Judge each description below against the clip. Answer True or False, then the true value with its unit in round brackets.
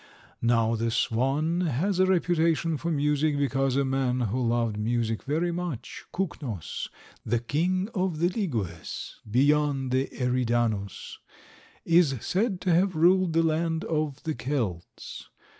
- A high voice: False (145 Hz)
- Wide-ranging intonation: True (5.9 semitones)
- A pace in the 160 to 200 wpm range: False (135 wpm)